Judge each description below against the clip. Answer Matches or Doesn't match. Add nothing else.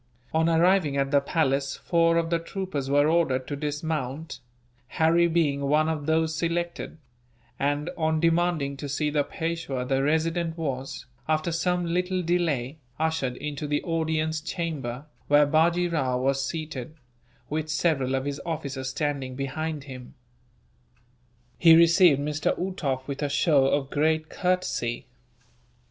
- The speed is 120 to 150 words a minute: Matches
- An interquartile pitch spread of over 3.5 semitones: Doesn't match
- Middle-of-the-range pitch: Matches